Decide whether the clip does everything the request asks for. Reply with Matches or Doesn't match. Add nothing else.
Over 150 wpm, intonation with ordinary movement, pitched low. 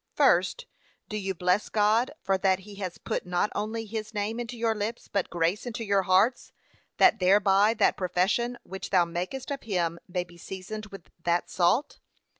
Doesn't match